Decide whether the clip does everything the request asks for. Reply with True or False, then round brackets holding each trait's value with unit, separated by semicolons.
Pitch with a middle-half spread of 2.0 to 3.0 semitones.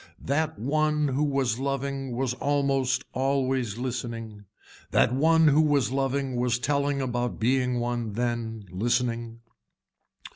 True (2.7 semitones)